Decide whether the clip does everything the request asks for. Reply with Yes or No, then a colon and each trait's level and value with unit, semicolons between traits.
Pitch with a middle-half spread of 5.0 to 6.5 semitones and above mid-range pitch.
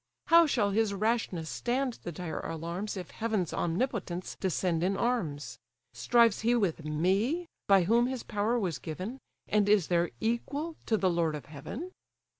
Yes: wide, 5.5 semitones; high, 200 Hz